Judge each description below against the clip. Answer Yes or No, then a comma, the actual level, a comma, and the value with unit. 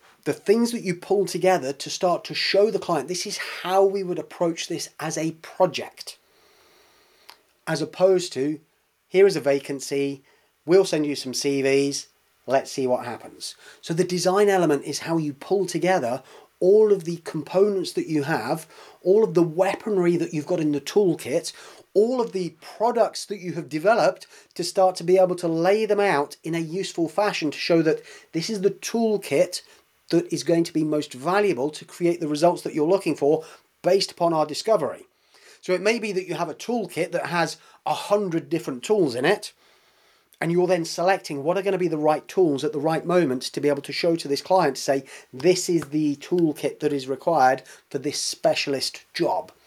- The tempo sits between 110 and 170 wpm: No, average, 195 wpm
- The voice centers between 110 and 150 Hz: No, medium, 175 Hz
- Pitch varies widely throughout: No, average, 4.1 semitones